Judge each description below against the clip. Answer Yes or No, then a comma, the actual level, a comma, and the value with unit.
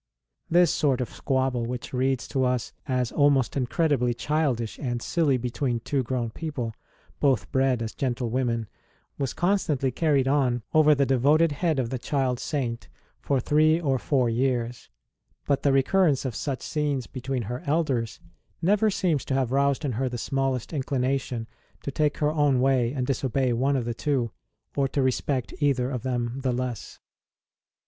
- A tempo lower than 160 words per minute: No, average, 170 wpm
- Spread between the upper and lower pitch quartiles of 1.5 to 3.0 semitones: Yes, narrow, 2.6 semitones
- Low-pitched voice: Yes, low, 130 Hz